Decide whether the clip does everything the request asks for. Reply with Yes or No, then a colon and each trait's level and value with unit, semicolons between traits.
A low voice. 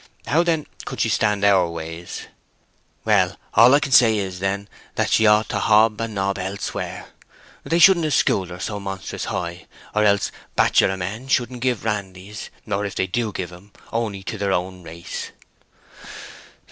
Yes: low, 100 Hz